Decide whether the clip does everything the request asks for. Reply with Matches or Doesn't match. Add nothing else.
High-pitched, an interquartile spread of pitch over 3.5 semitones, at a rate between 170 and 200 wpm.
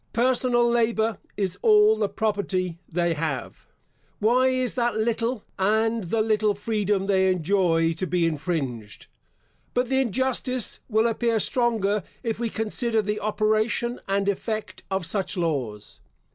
Doesn't match